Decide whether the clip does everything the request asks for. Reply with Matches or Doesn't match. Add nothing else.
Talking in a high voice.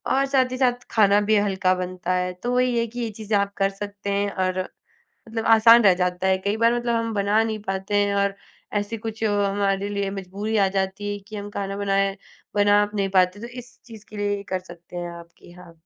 Matches